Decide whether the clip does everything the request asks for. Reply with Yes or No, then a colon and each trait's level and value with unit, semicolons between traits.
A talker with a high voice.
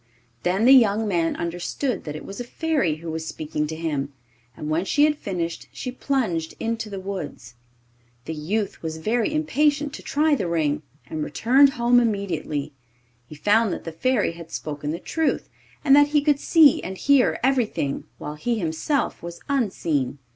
Yes: high, 195 Hz